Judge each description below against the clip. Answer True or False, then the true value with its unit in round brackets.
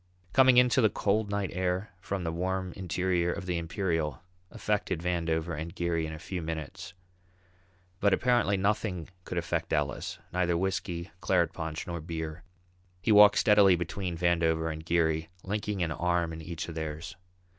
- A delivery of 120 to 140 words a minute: False (165 wpm)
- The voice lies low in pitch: True (85 Hz)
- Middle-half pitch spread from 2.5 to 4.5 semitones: True (2.8 semitones)